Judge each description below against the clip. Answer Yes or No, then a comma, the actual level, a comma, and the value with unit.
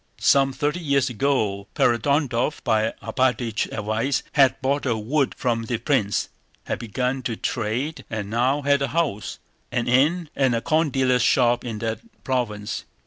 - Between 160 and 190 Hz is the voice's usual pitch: No, low, 125 Hz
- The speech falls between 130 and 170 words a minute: Yes, average, 155 wpm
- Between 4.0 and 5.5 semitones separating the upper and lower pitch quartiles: No, average, 3.6 semitones